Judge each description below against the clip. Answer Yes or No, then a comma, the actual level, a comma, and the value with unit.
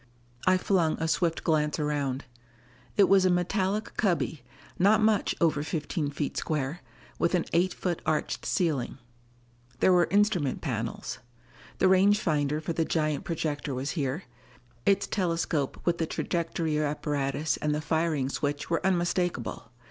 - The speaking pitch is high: No, medium, 160 Hz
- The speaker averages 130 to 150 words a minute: Yes, average, 145 wpm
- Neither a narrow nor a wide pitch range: Yes, average, 3.6 semitones